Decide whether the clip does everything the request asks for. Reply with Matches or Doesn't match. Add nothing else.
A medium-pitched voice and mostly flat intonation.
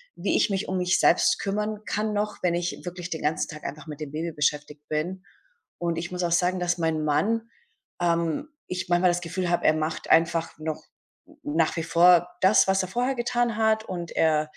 Doesn't match